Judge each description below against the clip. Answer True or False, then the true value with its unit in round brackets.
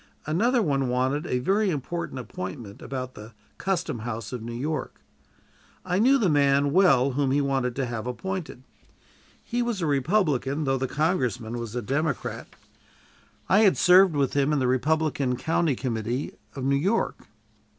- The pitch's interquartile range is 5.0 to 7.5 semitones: True (5.3 semitones)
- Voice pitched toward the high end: False (140 Hz)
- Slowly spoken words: False (160 wpm)